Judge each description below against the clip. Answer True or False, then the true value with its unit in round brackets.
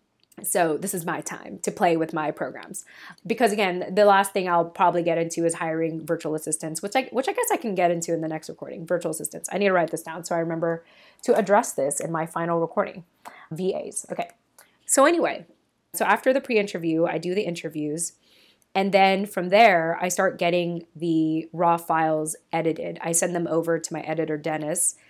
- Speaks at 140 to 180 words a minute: False (205 wpm)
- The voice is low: False (170 Hz)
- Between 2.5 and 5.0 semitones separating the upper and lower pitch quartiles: True (3.0 semitones)